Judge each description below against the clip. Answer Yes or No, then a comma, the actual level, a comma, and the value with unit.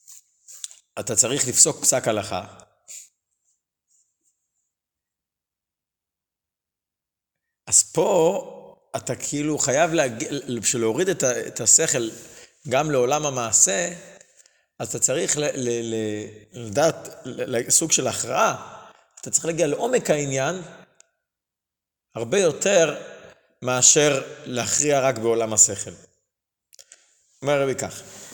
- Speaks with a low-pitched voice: Yes, low, 120 Hz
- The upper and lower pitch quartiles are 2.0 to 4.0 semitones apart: No, average, 4.5 semitones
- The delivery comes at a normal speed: No, slow, 85 wpm